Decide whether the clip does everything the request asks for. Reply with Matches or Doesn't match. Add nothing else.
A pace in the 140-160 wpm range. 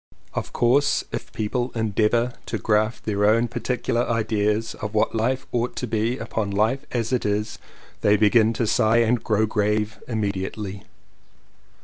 Matches